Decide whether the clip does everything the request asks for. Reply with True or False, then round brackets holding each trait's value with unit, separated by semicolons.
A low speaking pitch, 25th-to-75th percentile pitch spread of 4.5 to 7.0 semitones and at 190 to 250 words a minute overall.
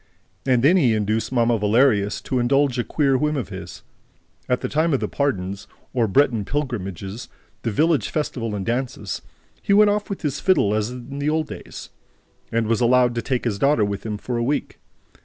True (125 Hz; 4.8 semitones; 195 wpm)